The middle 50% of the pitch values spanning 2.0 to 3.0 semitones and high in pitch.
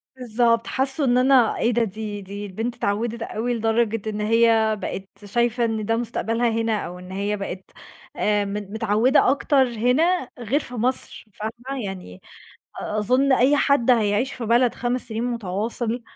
Yes: average, 2.7 semitones; high, 230 Hz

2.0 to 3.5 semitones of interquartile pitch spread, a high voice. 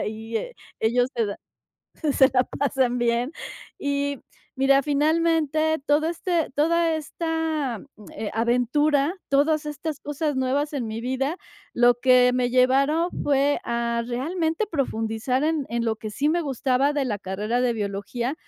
No: average, 4.2 semitones; very high, 275 Hz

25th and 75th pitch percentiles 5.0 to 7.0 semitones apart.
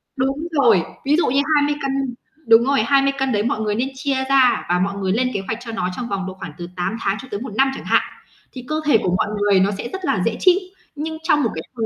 Yes: average, 5.3 semitones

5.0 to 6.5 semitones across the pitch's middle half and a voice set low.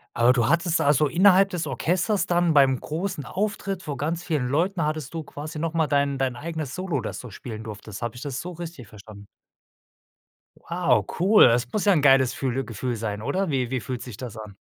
No: wide, 5.5 semitones; medium, 145 Hz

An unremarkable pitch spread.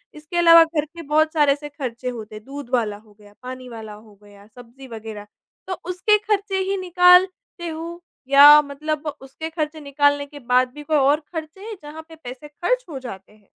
Yes: average, 4.8 semitones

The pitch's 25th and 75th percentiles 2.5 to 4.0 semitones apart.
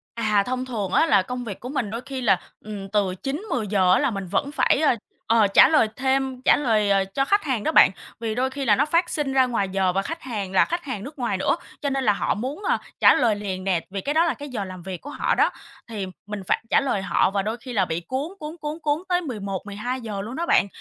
No: wide, 5.6 semitones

